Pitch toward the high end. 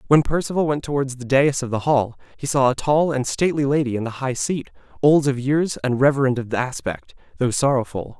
No: low, 135 Hz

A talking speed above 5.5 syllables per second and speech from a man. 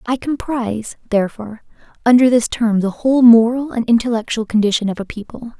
No: 5.9 syllables/s; female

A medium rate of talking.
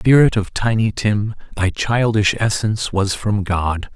Yes: average, 150 wpm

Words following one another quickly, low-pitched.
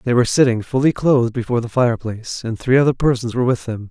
Yes: fast, 230 wpm; low, 120 Hz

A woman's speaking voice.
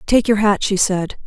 Yes: female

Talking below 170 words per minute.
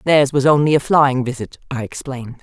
No: average, 200 wpm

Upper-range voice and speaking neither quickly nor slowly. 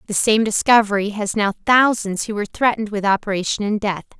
Yes: high, 210 Hz; average, 185 wpm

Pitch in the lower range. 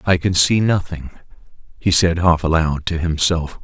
Yes: very low, 85 Hz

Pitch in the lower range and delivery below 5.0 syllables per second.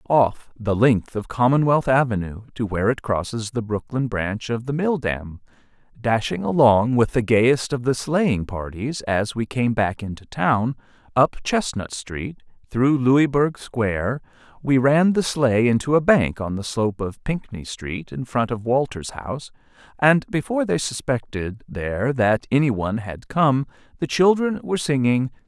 Yes: low, 125 Hz; 4.5 syllables/s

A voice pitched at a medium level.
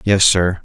No: very low, 95 Hz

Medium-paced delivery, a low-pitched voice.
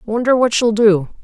No: average, 195 wpm; high, 220 Hz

